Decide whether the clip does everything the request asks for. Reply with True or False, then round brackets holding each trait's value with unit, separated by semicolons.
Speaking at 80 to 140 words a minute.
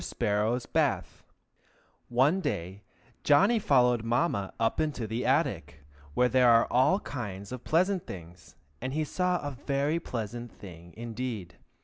True (135 wpm)